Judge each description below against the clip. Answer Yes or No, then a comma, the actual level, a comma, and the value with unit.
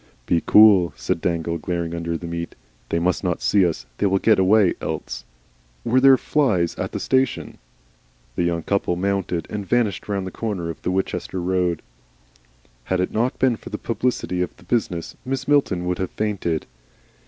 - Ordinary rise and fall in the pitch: Yes, average, 4.0 semitones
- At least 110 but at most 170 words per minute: No, average, 180 wpm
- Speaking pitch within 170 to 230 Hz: No, very low, 95 Hz